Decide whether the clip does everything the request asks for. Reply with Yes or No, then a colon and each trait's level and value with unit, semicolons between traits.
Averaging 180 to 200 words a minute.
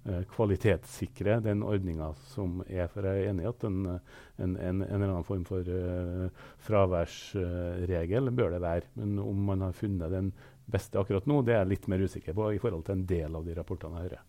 Yes: average, 195 wpm